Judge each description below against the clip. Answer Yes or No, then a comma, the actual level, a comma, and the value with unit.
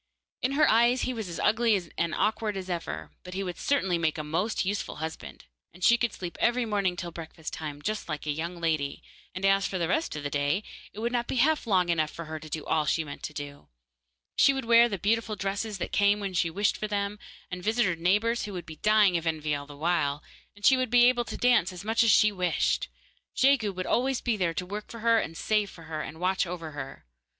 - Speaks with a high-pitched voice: Yes, high, 195 Hz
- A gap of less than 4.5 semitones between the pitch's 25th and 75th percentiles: No, average, 5.3 semitones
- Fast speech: Yes, fast, 240 wpm